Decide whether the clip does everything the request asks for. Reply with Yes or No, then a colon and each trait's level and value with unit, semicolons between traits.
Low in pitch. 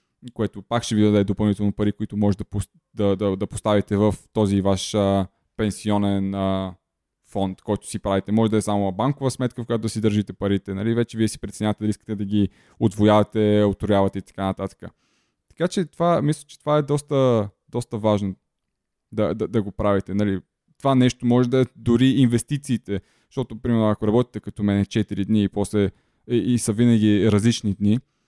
Yes: low, 105 Hz